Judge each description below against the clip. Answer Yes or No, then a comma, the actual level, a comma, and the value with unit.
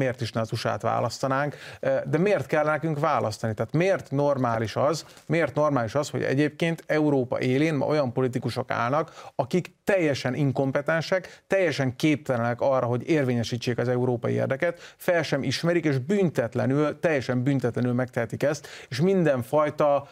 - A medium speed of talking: Yes, average, 145 wpm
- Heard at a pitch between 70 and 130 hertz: No, medium, 140 Hz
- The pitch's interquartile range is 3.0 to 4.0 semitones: Yes, average, 3.7 semitones